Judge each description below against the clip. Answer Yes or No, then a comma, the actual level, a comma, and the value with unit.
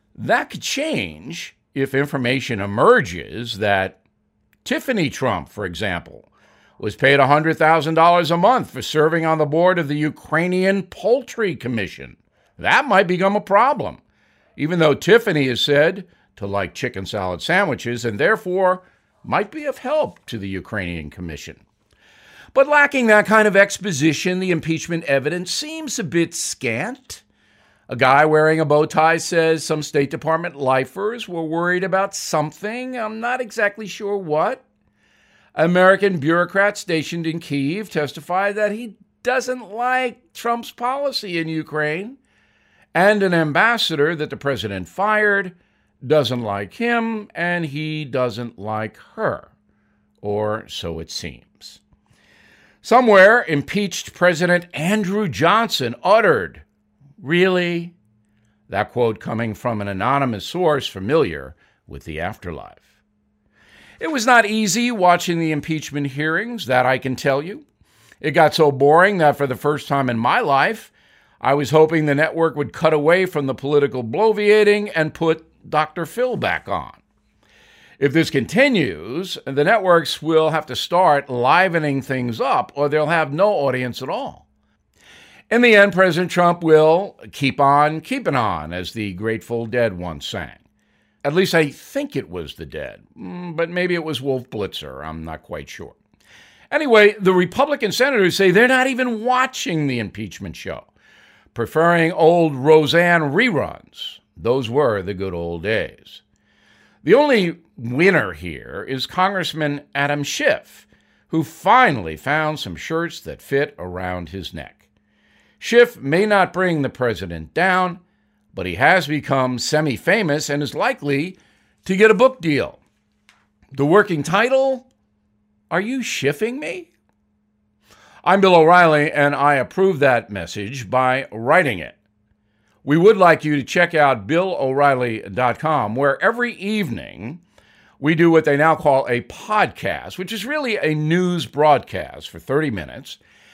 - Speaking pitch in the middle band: Yes, medium, 155 Hz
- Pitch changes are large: Yes, wide, 6.9 semitones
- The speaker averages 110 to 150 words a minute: Yes, average, 140 wpm